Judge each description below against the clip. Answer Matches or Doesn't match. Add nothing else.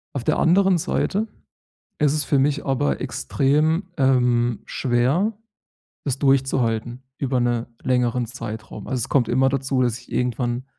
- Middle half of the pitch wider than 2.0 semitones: Matches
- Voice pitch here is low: Matches